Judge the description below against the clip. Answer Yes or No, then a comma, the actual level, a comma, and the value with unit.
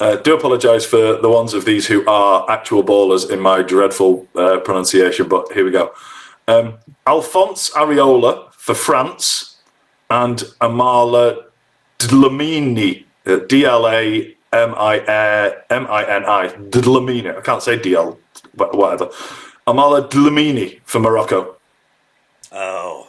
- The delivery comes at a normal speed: No, slow, 110 wpm